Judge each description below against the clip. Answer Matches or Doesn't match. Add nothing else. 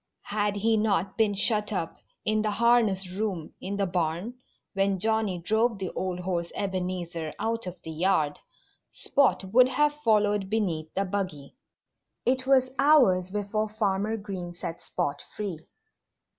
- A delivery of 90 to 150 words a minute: Matches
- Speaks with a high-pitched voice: Matches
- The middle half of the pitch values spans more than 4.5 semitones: Doesn't match